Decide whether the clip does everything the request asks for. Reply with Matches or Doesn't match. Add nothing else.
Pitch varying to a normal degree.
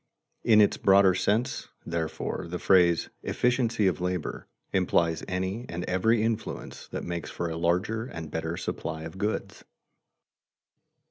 Matches